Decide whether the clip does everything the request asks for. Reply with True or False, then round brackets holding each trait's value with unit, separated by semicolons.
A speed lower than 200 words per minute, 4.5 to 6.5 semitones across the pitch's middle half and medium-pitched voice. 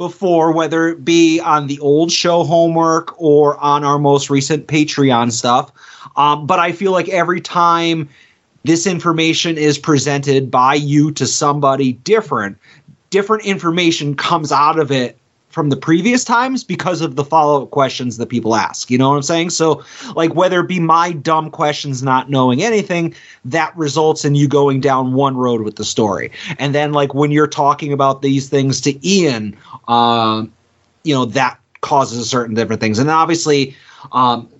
False (175 wpm; 3.5 semitones; 150 Hz)